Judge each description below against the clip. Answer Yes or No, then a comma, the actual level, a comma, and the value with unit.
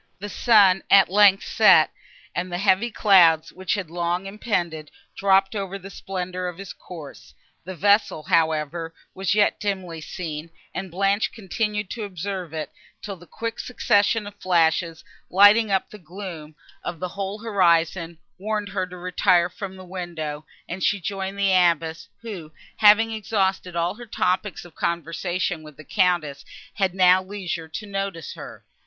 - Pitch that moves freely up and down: No, average, 2.9 semitones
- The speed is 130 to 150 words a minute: No, average, 160 wpm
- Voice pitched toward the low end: No, medium, 185 Hz